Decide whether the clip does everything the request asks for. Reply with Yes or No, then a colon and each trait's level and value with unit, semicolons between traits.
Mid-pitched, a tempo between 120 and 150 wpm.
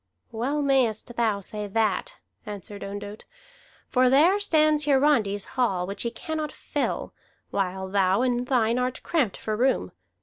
No: high, 235 Hz; average, 140 wpm